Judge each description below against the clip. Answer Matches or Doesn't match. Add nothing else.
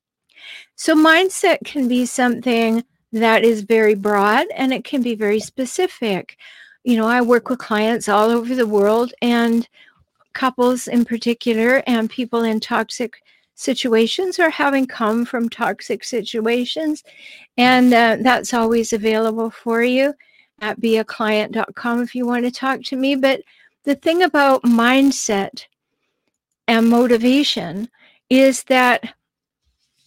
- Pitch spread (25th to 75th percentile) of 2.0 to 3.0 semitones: Matches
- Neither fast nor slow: Doesn't match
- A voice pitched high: Matches